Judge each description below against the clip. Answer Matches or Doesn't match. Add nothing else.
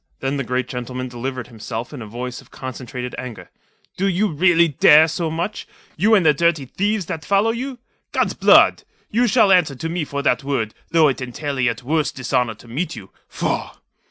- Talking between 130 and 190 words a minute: Doesn't match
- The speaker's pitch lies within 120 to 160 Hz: Matches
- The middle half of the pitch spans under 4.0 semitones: Doesn't match